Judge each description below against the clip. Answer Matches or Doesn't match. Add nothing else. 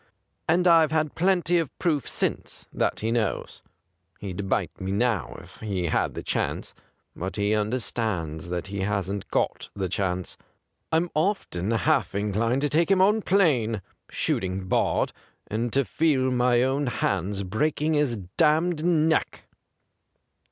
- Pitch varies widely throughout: Matches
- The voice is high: Doesn't match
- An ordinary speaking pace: Matches